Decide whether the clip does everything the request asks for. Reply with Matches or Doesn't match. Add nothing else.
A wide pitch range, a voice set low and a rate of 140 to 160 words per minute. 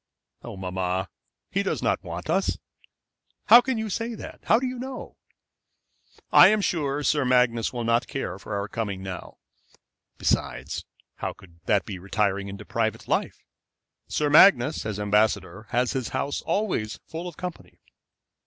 Matches